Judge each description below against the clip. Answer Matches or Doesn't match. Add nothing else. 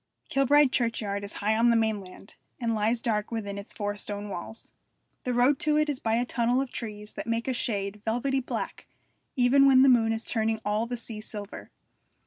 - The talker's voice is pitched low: Doesn't match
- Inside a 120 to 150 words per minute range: Doesn't match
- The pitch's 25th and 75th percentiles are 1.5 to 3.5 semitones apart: Matches